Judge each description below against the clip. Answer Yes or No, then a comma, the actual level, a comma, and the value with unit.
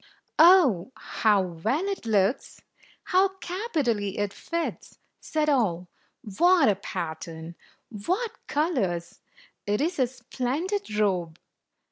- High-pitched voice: Yes, high, 240 Hz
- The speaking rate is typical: No, slow, 110 wpm